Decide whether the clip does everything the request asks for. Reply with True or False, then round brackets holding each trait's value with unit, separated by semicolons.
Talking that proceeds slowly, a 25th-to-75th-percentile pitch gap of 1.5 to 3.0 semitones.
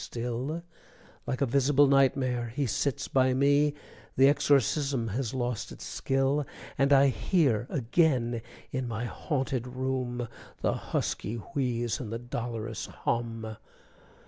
True (130 wpm; 2.7 semitones)